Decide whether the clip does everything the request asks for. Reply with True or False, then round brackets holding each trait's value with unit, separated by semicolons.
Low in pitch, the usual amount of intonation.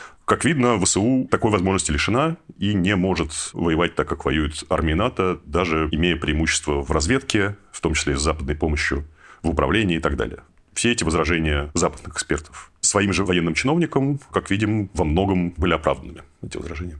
True (90 Hz; 4.4 semitones)